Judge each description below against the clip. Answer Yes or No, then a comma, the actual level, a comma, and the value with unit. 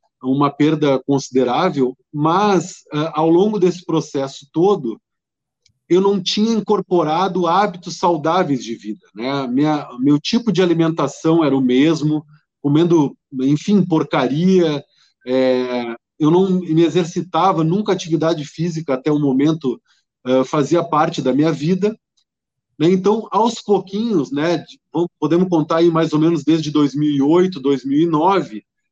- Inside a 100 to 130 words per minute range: Yes, average, 125 wpm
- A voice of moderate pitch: Yes, medium, 160 Hz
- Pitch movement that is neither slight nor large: Yes, average, 4.0 semitones